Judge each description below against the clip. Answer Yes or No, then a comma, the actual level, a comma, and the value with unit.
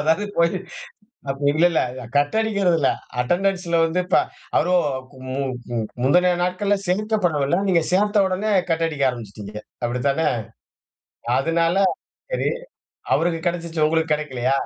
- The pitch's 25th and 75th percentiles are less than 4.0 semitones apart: No, average, 4.3 semitones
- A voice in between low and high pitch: Yes, medium, 165 Hz